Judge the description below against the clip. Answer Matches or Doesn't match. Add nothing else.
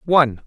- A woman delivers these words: Doesn't match